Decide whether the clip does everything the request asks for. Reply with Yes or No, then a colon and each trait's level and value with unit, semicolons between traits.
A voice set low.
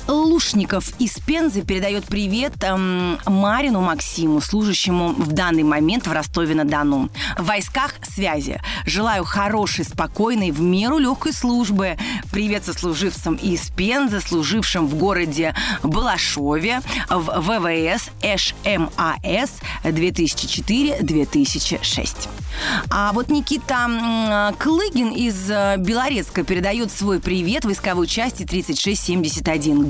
No: high, 195 Hz